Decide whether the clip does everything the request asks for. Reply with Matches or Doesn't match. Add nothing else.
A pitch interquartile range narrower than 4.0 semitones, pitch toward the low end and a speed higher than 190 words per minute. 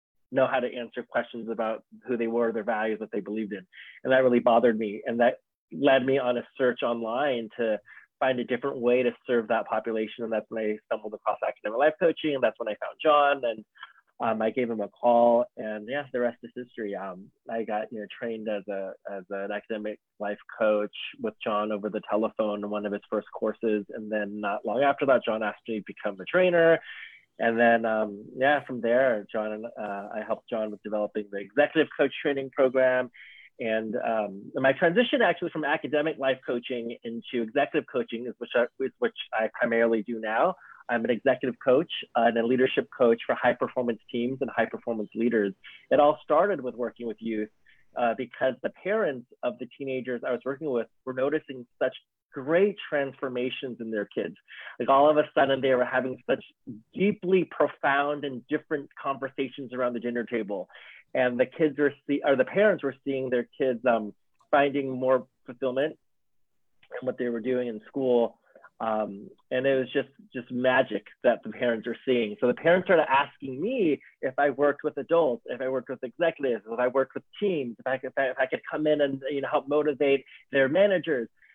Matches